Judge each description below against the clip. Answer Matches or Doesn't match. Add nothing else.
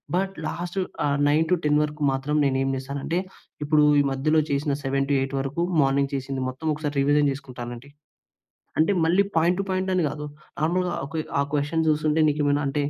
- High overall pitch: Doesn't match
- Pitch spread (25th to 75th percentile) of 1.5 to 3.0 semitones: Matches